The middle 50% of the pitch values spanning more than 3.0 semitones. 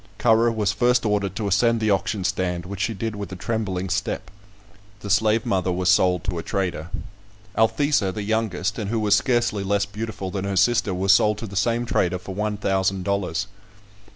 No: average, 2.7 semitones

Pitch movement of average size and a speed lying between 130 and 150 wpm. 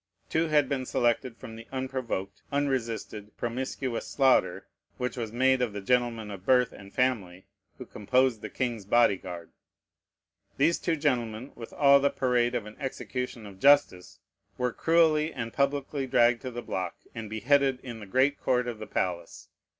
No: average, 3.5 semitones; average, 165 wpm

